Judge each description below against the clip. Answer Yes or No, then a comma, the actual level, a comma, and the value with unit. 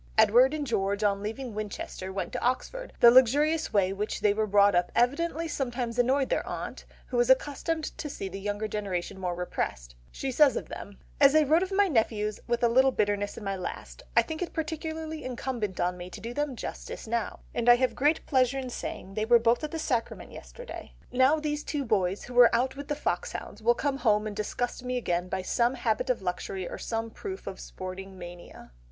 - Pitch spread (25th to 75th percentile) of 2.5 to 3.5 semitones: No, average, 5.2 semitones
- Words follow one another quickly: Yes, fast, 215 wpm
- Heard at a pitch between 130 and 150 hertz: No, high, 235 Hz